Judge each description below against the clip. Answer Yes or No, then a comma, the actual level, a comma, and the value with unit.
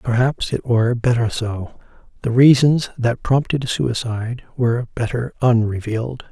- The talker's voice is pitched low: Yes, low, 120 Hz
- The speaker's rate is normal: No, slow, 125 wpm